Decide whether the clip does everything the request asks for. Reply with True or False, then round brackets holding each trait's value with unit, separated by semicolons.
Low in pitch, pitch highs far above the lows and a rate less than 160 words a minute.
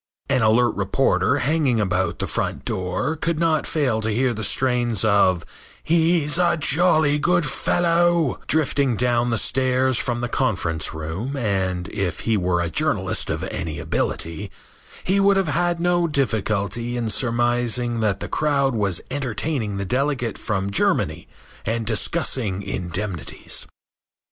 True (120 Hz; 6.5 semitones; 140 wpm)